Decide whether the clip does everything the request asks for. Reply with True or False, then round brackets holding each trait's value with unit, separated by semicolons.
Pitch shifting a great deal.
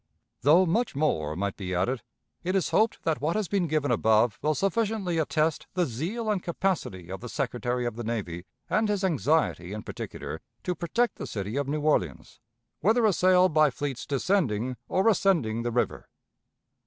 True (8.0 semitones)